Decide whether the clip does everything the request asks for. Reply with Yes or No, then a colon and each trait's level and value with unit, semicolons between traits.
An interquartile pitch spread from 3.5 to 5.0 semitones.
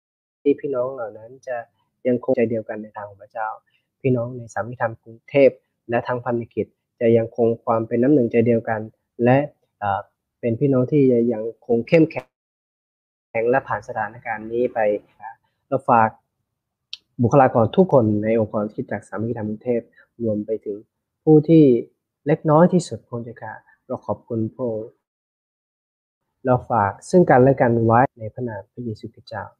No: narrow, 2.4 semitones